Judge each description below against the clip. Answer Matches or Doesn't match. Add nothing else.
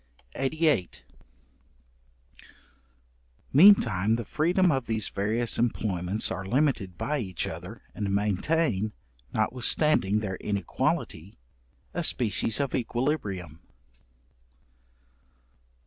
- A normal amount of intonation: Doesn't match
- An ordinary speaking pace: Doesn't match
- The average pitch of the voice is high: Doesn't match